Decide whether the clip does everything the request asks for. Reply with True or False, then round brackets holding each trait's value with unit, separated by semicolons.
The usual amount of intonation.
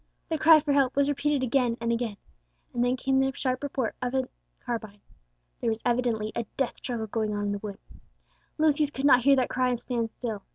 True (3.1 semitones)